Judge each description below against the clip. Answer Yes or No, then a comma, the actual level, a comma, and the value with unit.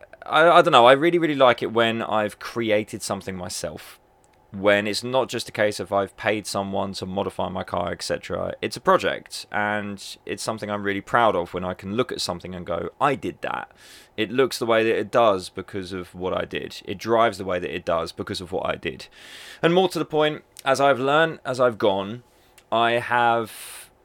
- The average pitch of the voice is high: No, low, 105 Hz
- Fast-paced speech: Yes, fast, 215 wpm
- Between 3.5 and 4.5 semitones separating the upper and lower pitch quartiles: Yes, average, 3.9 semitones